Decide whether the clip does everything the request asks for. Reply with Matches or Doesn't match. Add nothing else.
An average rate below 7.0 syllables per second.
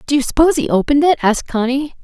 Doesn't match